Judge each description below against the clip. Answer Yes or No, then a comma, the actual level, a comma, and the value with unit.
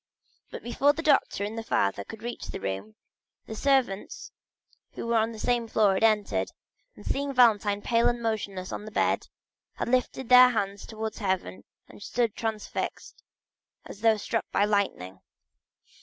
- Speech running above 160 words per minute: Yes, average, 170 wpm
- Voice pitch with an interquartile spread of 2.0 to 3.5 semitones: Yes, average, 2.9 semitones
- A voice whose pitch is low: No, high, 220 Hz